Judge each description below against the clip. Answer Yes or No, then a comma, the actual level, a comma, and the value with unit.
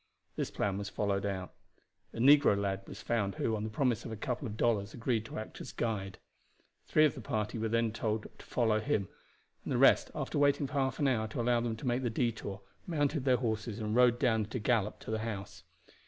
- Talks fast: Yes, fast, 235 wpm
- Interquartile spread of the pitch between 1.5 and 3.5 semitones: Yes, average, 2.9 semitones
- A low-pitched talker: Yes, low, 115 Hz